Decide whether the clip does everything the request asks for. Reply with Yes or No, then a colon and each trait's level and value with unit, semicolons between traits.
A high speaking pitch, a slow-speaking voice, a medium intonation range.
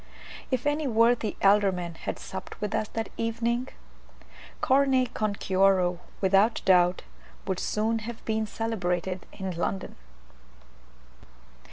Yes: high, 215 Hz; slow, 115 wpm; average, 3.4 semitones